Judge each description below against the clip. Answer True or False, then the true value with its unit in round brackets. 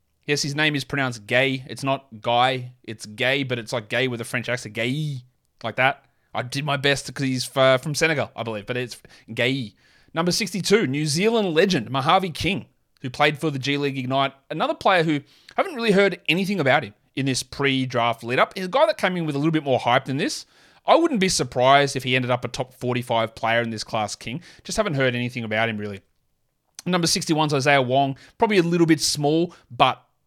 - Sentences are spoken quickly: True (220 wpm)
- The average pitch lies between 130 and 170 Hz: True (135 Hz)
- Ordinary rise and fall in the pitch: True (4.1 semitones)